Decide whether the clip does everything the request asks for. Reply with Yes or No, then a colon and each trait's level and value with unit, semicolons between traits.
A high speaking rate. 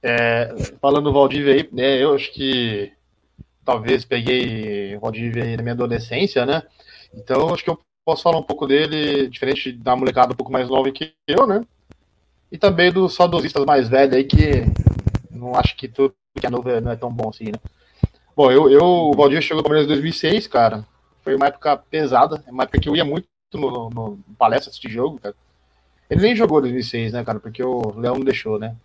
Yes: fast, 200 wpm